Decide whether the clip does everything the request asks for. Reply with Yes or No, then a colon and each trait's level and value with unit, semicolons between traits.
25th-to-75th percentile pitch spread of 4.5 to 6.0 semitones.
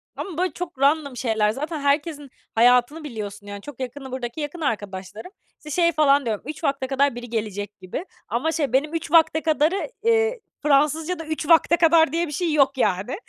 Yes: average, 5.0 semitones